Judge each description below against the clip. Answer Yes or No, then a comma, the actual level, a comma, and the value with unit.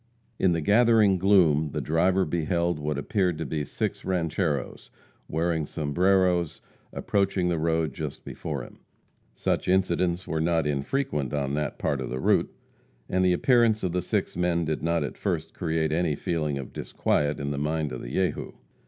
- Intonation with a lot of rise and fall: No, average, 3.4 semitones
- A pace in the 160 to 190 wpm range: Yes, average, 170 wpm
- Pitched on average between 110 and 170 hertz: No, very low, 85 Hz